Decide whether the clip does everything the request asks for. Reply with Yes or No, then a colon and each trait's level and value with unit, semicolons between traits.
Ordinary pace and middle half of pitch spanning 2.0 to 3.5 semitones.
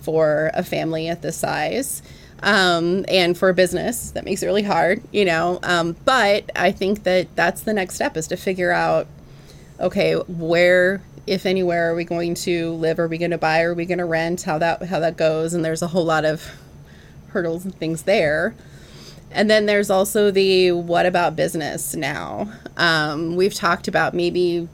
Yes: average, 190 wpm; narrow, 2.4 semitones